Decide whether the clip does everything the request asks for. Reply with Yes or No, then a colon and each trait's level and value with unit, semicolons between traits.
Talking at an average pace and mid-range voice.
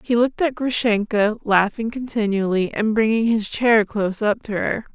No: average, 170 wpm; high, 220 Hz